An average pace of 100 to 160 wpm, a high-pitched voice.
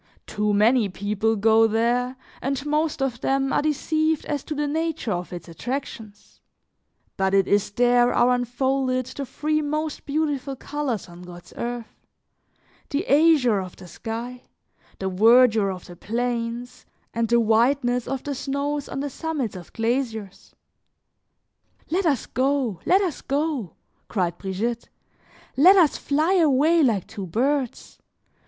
Yes: average, 145 wpm; very high, 250 Hz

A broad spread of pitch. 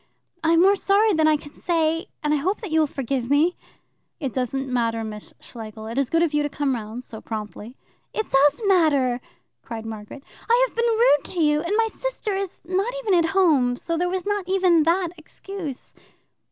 Yes: wide, 6.7 semitones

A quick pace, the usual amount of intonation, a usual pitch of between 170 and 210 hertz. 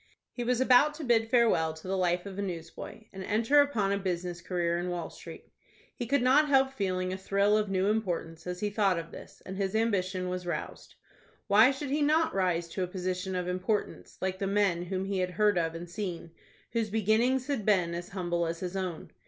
Yes: fast, 220 wpm; average, 3.7 semitones; high, 190 Hz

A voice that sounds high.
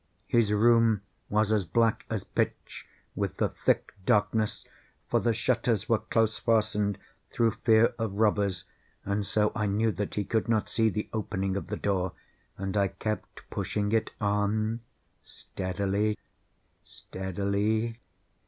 No: low, 105 Hz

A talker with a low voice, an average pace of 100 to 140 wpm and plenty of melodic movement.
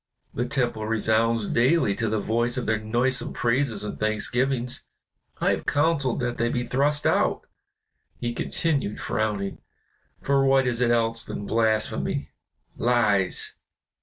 No: low, 120 Hz; slow, 135 wpm; average, 2.7 semitones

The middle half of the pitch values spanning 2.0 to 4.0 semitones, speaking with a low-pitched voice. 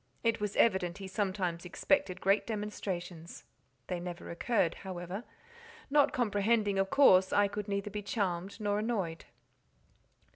No: narrow, 2.6 semitones; high, 200 Hz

